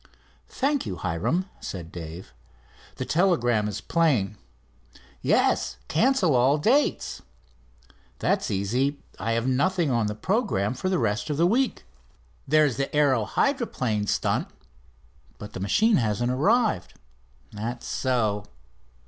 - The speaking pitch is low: Yes, low, 130 Hz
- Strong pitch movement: Yes, wide, 8.9 semitones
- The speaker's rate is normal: No, slow, 125 wpm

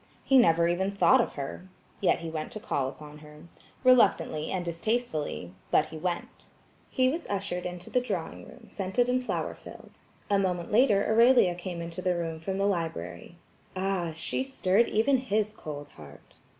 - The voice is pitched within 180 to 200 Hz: Yes, medium, 185 Hz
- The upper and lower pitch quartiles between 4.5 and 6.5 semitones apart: Yes, average, 5.1 semitones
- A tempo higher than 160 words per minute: Yes, average, 170 wpm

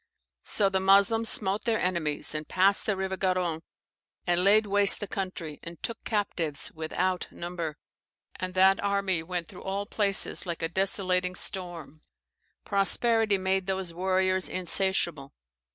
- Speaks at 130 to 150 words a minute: Yes, average, 140 wpm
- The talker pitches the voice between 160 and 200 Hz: Yes, high, 190 Hz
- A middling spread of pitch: No, narrow, 2.2 semitones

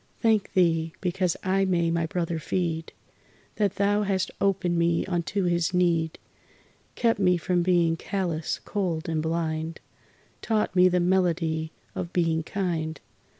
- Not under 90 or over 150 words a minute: Yes, average, 140 wpm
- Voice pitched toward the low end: No, medium, 175 Hz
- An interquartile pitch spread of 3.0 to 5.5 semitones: No, narrow, 2.4 semitones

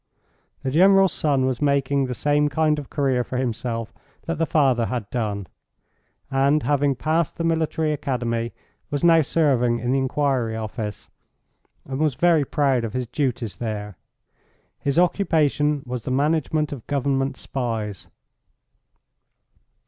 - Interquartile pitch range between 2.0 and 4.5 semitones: Yes, average, 3.6 semitones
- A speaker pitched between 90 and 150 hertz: Yes, low, 135 Hz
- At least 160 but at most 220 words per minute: No, average, 140 wpm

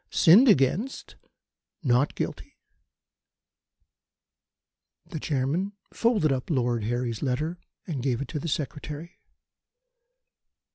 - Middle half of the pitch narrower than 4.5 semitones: No, average, 5.0 semitones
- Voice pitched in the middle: Yes, medium, 145 Hz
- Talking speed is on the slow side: Yes, slow, 95 wpm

